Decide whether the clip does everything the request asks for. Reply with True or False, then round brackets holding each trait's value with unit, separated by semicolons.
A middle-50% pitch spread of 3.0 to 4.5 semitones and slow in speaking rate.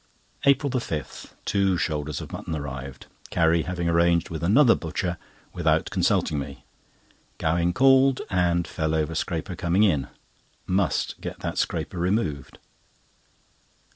True (3.7 semitones; 120 wpm)